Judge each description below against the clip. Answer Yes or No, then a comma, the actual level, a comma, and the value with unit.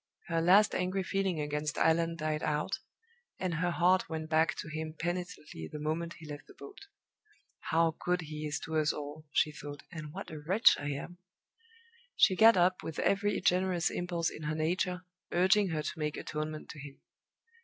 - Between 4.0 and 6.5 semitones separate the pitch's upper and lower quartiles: No, average, 2.9 semitones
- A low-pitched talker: No, medium, 165 Hz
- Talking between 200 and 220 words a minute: No, average, 185 wpm